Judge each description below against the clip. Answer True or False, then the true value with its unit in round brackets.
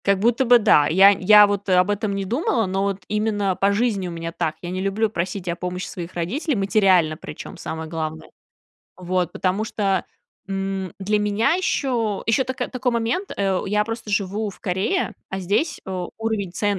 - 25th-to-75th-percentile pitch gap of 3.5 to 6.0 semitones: False (3.0 semitones)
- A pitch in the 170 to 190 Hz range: False (200 Hz)